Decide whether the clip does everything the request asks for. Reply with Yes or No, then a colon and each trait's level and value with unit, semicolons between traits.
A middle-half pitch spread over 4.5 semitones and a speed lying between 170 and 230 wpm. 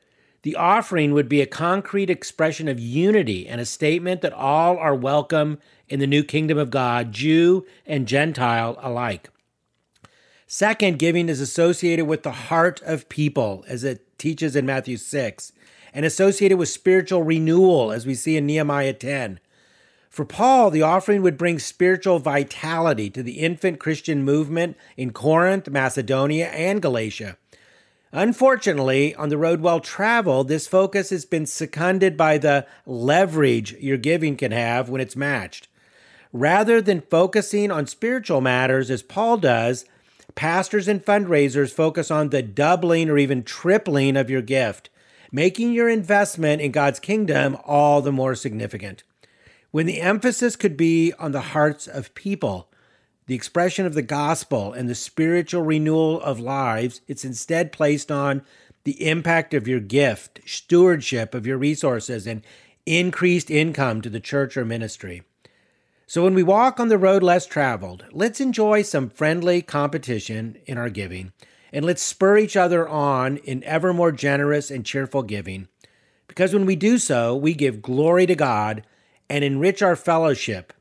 No: average, 4.9 semitones; average, 155 wpm